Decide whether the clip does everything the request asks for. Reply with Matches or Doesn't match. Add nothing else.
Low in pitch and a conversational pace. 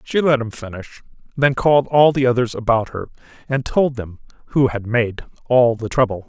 Matches